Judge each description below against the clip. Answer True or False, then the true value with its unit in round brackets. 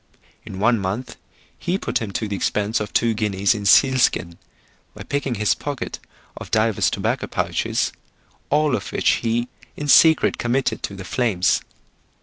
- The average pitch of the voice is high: False (115 Hz)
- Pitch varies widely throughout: False (4.3 semitones)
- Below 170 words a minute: True (160 wpm)